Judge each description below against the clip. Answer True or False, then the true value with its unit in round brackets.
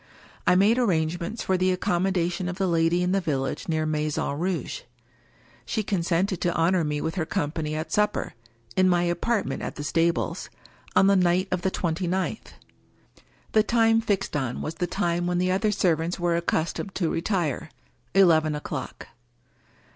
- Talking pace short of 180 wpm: True (170 wpm)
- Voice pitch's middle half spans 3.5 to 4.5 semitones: False (2.7 semitones)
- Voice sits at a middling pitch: True (175 Hz)